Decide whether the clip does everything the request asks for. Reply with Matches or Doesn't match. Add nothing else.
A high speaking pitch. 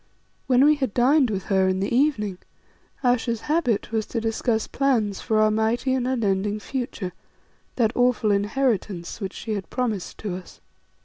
Matches